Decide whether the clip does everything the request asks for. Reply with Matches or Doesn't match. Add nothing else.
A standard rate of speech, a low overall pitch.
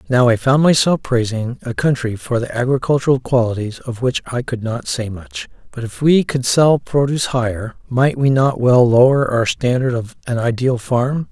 Matches